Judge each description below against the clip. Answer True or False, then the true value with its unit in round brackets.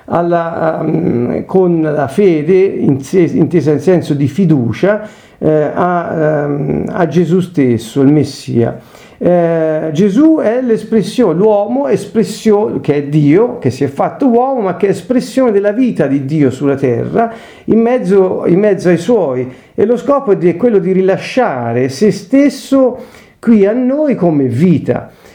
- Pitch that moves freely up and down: True (6.2 semitones)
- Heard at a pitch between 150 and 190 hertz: True (185 Hz)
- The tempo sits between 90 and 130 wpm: False (160 wpm)